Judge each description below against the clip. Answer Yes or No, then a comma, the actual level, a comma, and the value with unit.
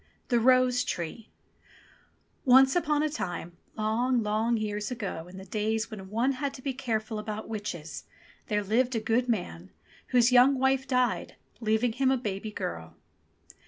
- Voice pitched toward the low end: No, high, 225 Hz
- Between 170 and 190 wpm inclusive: No, average, 160 wpm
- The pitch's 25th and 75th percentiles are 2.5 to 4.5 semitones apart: Yes, average, 3.4 semitones